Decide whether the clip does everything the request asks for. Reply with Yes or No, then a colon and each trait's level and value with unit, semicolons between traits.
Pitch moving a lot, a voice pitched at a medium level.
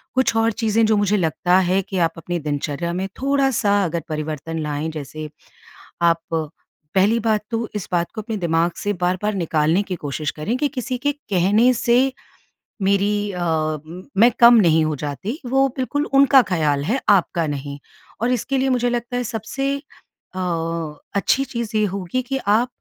No: wide, 6.3 semitones; high, 200 Hz